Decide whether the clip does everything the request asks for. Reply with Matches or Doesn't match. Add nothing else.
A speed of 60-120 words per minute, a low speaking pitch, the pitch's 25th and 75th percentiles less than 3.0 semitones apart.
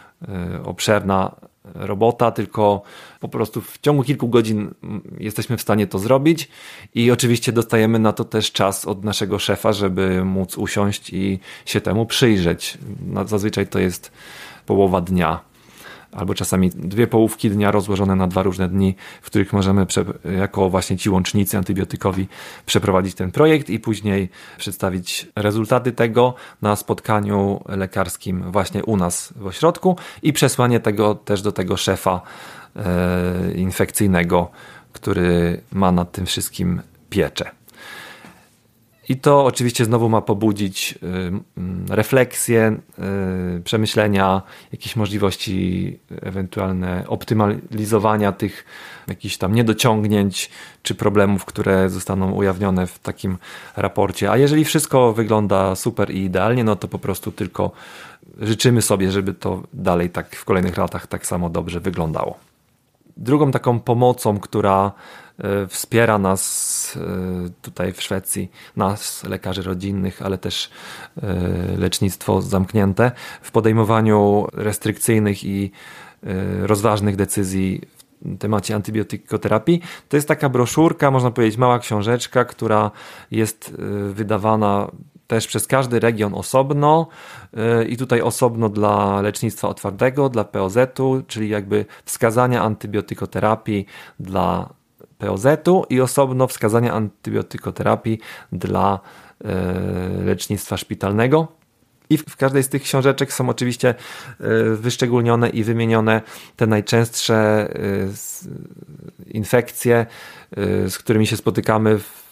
Doesn't match